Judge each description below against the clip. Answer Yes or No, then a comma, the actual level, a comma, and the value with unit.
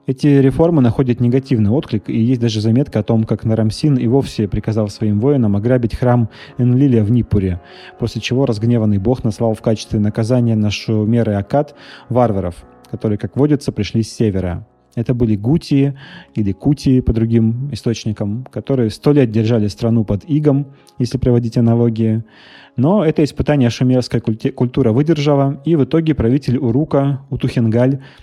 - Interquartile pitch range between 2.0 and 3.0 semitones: No, average, 3.6 semitones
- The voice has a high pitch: No, low, 120 Hz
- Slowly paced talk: No, average, 155 wpm